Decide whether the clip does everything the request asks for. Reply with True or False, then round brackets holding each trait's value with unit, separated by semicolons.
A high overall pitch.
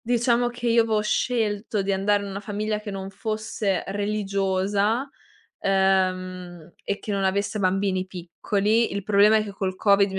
True (200 Hz)